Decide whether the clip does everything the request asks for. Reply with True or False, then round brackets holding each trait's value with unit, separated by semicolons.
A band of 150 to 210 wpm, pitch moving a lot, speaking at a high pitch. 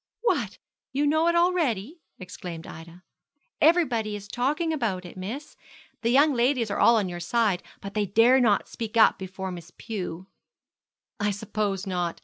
True (165 wpm; 5.9 semitones; 215 Hz)